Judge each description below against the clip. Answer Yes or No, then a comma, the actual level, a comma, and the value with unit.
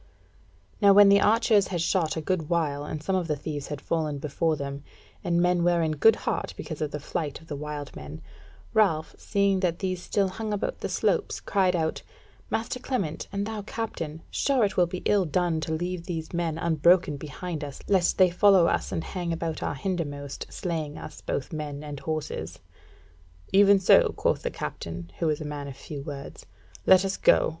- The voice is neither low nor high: Yes, medium, 165 Hz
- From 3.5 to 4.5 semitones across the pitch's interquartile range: Yes, average, 4.0 semitones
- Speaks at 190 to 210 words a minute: Yes, average, 200 wpm